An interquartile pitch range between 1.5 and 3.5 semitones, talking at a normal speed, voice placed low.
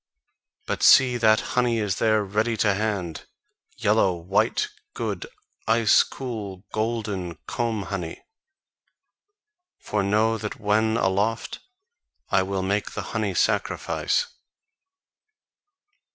No: narrow, 2.5 semitones; slow, 105 wpm; low, 105 Hz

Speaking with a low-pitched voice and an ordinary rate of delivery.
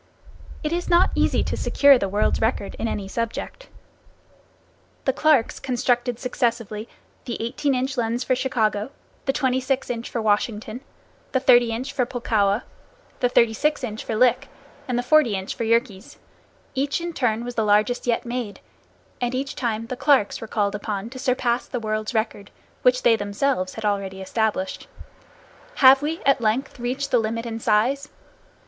No: high, 240 Hz; average, 165 wpm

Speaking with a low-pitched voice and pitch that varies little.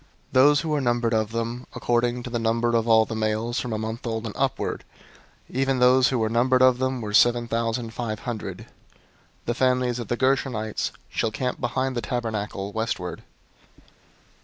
Yes: low, 120 Hz; narrow, 2.2 semitones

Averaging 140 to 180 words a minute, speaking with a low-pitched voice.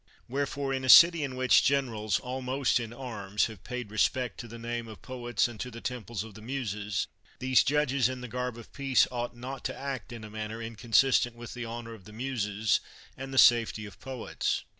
No: fast, 205 wpm; low, 120 Hz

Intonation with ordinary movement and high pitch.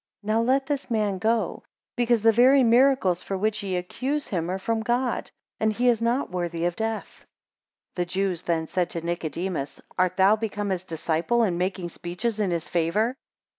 Yes: average, 4.8 semitones; high, 200 Hz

